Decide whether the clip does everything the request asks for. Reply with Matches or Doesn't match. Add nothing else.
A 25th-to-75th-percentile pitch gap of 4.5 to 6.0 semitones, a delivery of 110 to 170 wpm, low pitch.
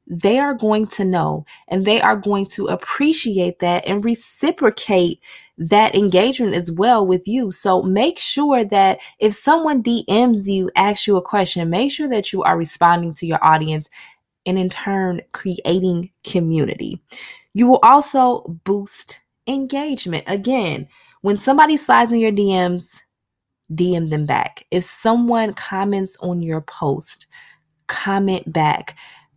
Doesn't match